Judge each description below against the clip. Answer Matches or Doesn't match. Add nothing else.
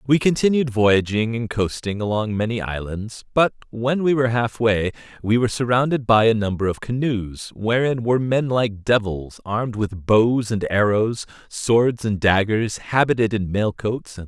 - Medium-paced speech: Matches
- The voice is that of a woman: Doesn't match